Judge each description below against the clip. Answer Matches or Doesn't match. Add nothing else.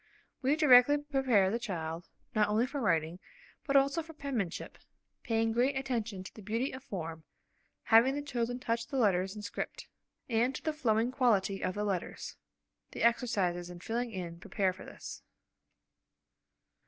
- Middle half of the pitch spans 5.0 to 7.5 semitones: Matches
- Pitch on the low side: Doesn't match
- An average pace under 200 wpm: Matches